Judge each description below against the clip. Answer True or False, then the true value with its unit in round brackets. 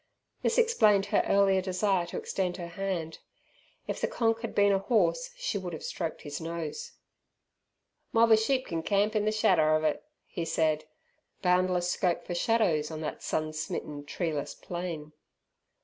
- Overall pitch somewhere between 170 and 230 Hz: True (185 Hz)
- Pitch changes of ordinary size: True (4.7 semitones)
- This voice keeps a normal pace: True (165 wpm)